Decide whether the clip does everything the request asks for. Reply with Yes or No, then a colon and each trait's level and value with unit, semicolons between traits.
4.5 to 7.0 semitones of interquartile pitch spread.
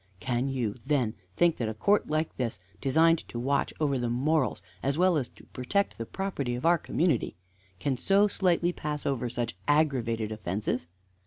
Yes: average, 5.3 semitones